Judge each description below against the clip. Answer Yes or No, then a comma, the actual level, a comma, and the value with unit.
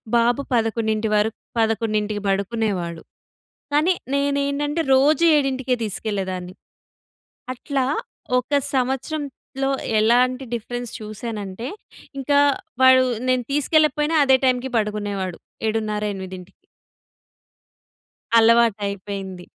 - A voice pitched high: Yes, high, 230 Hz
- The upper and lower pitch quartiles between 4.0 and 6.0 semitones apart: Yes, average, 4.3 semitones